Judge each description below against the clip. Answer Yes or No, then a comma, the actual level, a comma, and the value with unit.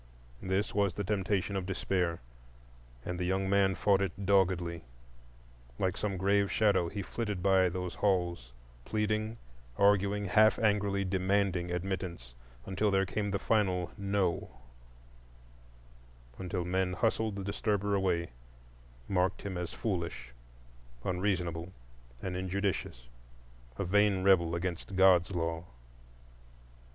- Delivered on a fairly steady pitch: Yes, narrow, 2.1 semitones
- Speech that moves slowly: Yes, slow, 120 wpm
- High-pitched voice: No, very low, 95 Hz